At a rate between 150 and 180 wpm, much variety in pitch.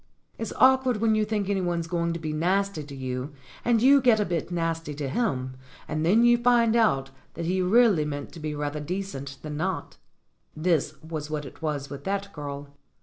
No: average, 200 wpm; wide, 6.1 semitones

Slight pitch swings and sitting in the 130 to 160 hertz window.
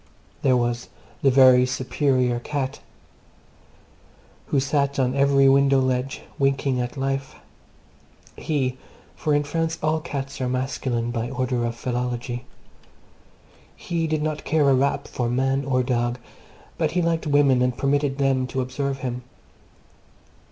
Yes: narrow, 1.9 semitones; low, 135 Hz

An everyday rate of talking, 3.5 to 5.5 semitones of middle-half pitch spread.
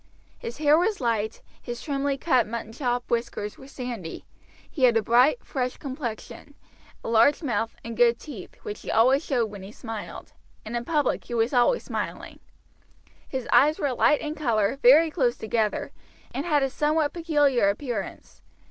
Yes: average, 165 wpm; average, 4.1 semitones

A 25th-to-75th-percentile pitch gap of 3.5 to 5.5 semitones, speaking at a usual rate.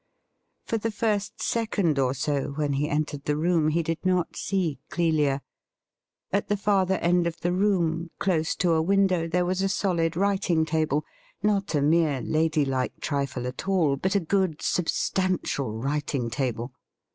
Yes: average, 4.3 semitones; average, 170 wpm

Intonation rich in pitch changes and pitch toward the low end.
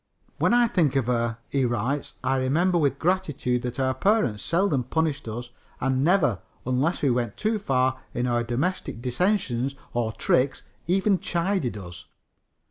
Yes: wide, 6.1 semitones; low, 130 Hz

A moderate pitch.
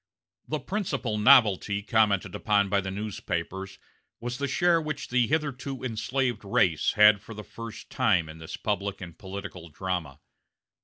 No: low, 105 Hz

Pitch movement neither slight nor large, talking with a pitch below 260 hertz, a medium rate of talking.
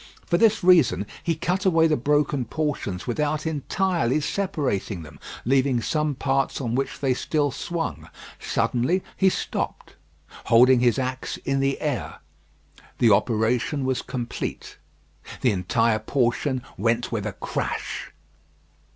No: average, 4.6 semitones; low, 135 Hz; slow, 130 wpm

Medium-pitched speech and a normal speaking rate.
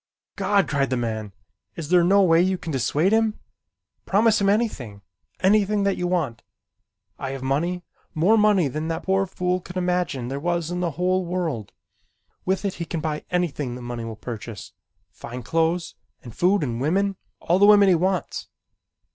Yes: medium, 175 Hz; average, 180 wpm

